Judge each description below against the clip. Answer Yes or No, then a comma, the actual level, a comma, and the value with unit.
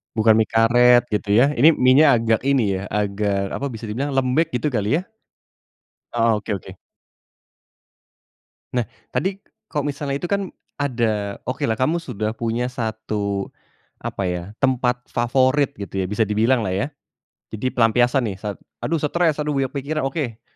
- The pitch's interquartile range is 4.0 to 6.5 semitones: Yes, average, 4.4 semitones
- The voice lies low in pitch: Yes, low, 120 Hz